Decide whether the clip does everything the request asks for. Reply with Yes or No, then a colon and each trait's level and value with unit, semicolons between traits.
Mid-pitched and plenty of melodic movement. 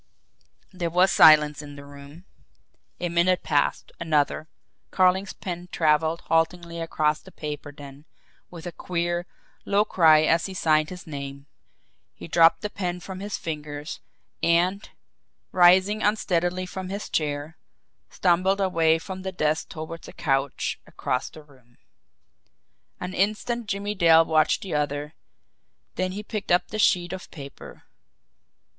No: medium, 170 Hz; average, 3.4 semitones